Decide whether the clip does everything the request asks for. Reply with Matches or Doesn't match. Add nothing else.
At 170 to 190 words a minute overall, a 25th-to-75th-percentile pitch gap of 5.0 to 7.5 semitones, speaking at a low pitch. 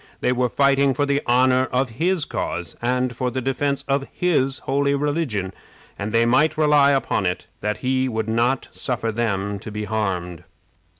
Doesn't match